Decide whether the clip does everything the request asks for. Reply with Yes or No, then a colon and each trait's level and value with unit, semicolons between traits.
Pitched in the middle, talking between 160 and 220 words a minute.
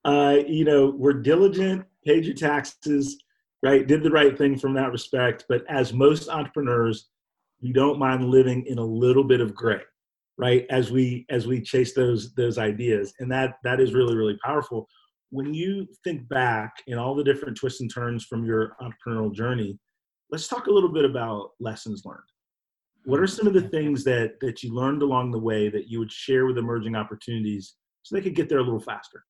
No: low, 130 Hz; average, 200 wpm